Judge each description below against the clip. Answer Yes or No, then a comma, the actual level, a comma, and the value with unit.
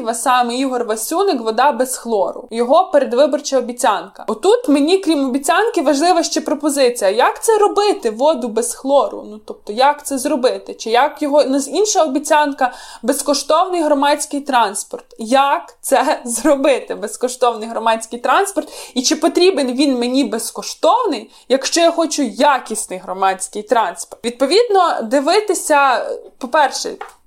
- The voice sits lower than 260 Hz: No, very high, 285 Hz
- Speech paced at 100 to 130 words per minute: Yes, average, 125 wpm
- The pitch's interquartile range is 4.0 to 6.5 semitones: Yes, average, 4.4 semitones